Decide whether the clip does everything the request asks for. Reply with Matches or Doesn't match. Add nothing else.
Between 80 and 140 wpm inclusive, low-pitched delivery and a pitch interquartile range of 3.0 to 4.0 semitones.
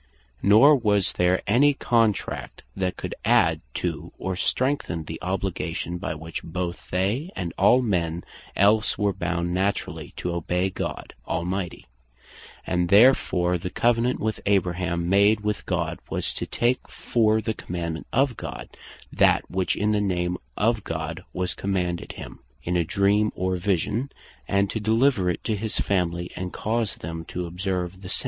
Doesn't match